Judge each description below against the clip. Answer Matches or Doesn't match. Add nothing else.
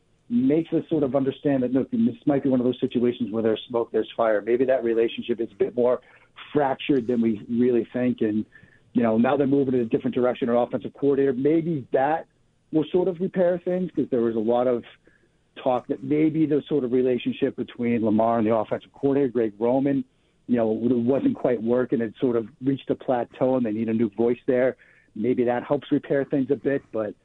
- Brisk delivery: Matches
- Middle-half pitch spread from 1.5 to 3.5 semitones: Matches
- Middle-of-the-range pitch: Doesn't match